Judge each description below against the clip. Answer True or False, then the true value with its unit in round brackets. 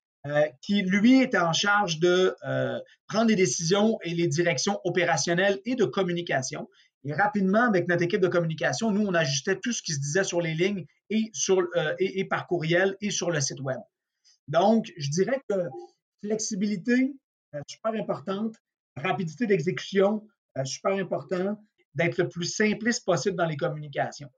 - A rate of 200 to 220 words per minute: False (170 wpm)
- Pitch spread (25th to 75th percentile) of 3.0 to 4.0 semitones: True (3.5 semitones)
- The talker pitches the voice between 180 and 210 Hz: True (185 Hz)